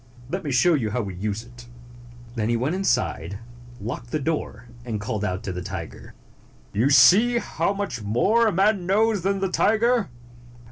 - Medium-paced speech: Yes, average, 175 wpm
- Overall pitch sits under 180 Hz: Yes, low, 135 Hz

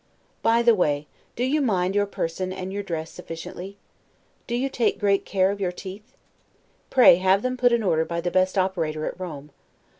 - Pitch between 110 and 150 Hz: No, high, 190 Hz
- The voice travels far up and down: No, average, 4.0 semitones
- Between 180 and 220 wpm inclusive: Yes, average, 190 wpm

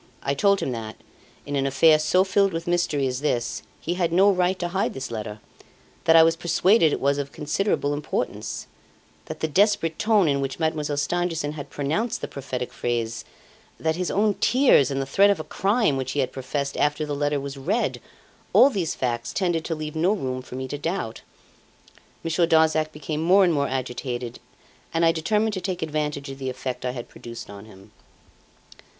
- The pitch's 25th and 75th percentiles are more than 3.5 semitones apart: Yes, average, 4.5 semitones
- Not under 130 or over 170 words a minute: No, average, 195 wpm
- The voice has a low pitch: No, medium, 155 Hz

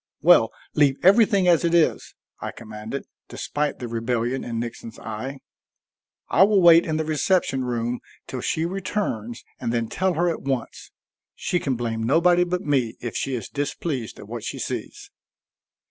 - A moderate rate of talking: Yes, average, 165 wpm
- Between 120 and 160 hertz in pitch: Yes, low, 135 Hz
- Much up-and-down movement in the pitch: Yes, wide, 6.5 semitones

